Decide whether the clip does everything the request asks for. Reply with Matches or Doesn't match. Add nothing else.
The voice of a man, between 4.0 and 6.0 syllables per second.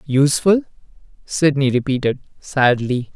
Matches